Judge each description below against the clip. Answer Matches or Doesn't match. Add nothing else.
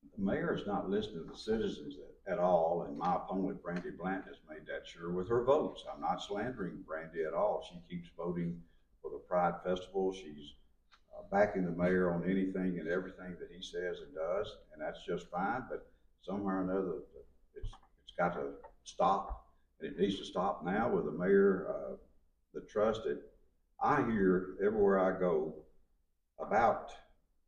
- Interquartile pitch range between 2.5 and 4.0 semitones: Matches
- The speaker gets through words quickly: Doesn't match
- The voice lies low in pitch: Matches